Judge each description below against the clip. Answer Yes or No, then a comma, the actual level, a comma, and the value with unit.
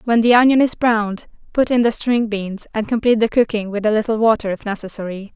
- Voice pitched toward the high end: Yes, high, 220 Hz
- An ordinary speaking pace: No, fast, 225 wpm